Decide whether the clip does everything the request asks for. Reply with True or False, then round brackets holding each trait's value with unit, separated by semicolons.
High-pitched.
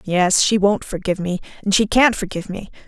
True (195 Hz)